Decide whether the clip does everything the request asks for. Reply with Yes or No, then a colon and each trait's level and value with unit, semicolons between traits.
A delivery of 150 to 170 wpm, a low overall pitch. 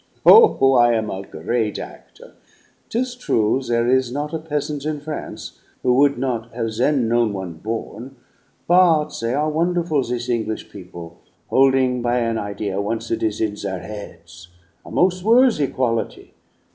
Yes: average, 160 wpm; low, 120 Hz